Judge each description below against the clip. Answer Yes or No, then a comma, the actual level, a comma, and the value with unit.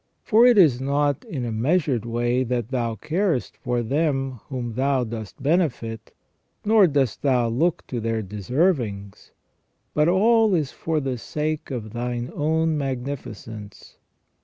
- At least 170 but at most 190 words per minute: No, average, 145 wpm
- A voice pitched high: No, low, 130 Hz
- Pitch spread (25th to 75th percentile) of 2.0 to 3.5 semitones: No, average, 4.8 semitones